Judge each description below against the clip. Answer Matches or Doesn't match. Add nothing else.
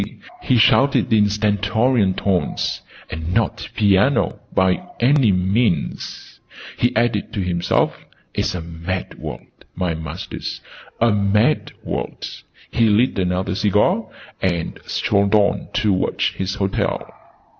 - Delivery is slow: Matches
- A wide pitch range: Doesn't match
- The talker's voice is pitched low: Matches